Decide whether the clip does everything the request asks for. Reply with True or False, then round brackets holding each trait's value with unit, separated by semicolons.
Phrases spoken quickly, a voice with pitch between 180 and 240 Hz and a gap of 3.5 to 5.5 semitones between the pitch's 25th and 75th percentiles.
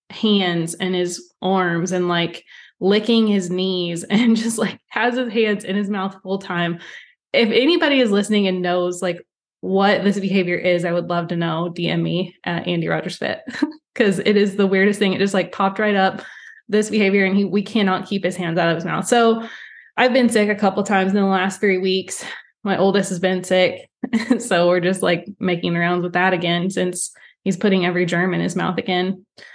False (210 wpm; 190 Hz; 2.7 semitones)